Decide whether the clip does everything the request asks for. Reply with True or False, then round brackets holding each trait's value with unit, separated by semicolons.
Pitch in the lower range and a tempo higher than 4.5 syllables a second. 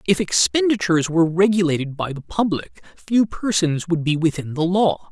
False (175 Hz; 5.3 syllables/s)